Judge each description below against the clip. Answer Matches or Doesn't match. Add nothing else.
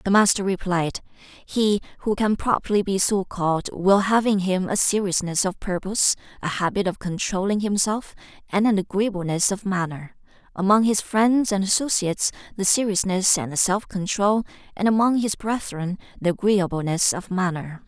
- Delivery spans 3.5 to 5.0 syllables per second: Matches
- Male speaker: Doesn't match